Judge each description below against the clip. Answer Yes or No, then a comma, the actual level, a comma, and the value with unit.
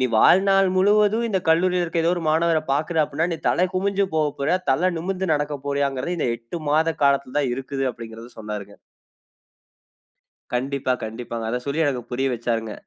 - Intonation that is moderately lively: No, wide, 5.7 semitones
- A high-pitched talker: No, medium, 145 Hz